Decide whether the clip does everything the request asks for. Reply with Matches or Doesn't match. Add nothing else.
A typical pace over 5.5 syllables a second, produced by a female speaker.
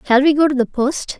Matches